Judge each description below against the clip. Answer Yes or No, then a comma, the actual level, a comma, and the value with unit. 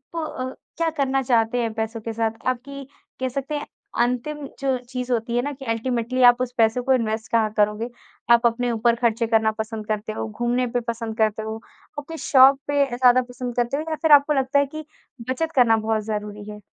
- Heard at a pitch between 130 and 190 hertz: No, high, 240 Hz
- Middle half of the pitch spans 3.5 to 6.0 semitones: No, average, 2.9 semitones